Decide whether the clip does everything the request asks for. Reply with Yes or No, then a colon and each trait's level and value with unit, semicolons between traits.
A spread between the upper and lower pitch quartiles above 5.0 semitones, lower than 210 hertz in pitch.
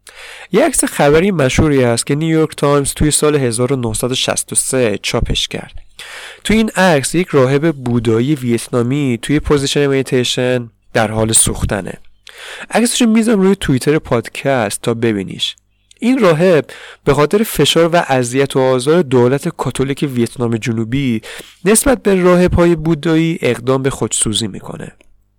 Yes: wide, 5.6 semitones; medium, 140 Hz